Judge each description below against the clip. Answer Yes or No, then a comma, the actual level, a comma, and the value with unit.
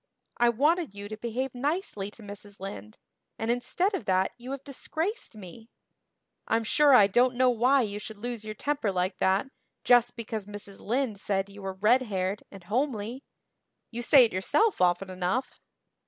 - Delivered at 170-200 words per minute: Yes, average, 175 wpm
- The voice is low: No, high, 225 Hz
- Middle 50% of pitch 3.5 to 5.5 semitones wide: Yes, average, 4.4 semitones